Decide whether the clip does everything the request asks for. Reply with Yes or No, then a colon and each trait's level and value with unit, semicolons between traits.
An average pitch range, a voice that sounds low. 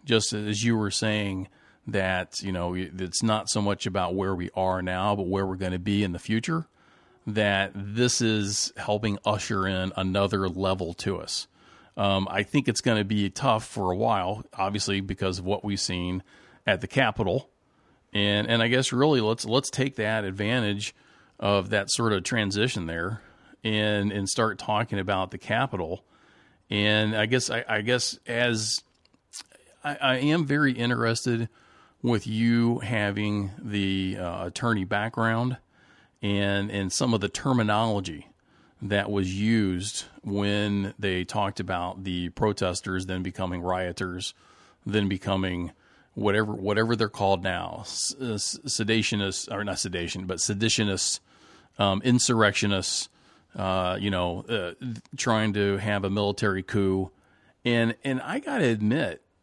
Yes: average, 3.0 semitones; low, 105 Hz